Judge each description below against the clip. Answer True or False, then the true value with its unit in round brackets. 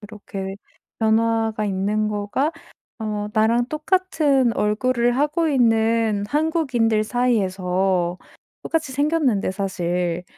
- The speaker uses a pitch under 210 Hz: False (225 Hz)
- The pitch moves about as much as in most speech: True (4.4 semitones)